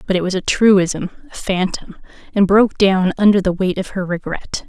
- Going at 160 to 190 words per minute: No, fast, 205 wpm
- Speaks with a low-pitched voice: No, high, 190 Hz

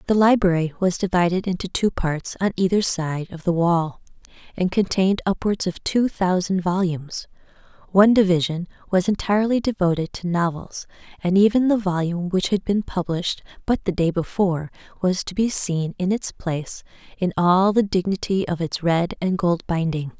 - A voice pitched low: No, medium, 185 Hz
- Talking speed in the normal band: Yes, average, 165 wpm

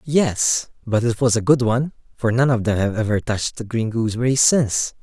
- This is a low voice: Yes, low, 120 Hz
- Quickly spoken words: Yes, fast, 215 wpm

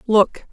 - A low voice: No, high, 215 Hz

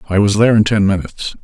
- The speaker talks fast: Yes, fast, 250 wpm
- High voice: No, low, 100 Hz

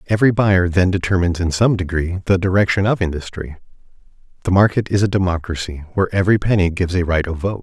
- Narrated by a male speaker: Yes, male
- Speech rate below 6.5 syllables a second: No, 6.7 syllables/s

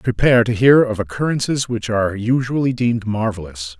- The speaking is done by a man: Yes, male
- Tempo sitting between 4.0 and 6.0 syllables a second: Yes, 5.6 syllables/s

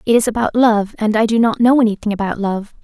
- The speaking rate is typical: No, fast, 255 wpm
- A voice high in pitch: Yes, high, 220 Hz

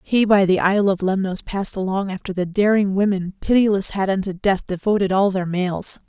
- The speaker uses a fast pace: No, average, 195 wpm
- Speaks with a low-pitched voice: No, high, 195 Hz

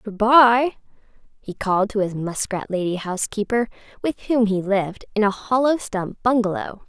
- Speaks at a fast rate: No, average, 155 wpm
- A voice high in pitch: Yes, high, 215 Hz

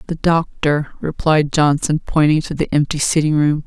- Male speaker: No, female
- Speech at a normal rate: Yes, average, 165 wpm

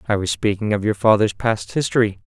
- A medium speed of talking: No, fast, 210 wpm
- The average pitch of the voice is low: Yes, low, 105 Hz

